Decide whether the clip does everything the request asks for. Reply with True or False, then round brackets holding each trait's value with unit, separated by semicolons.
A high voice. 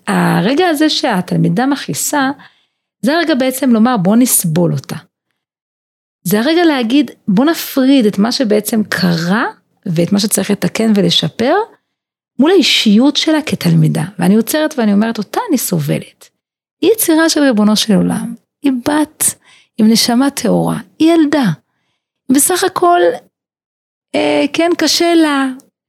True (250 Hz)